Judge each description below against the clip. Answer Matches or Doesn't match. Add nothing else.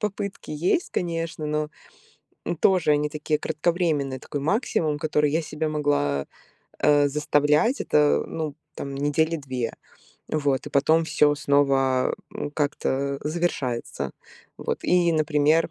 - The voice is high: Doesn't match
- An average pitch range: Doesn't match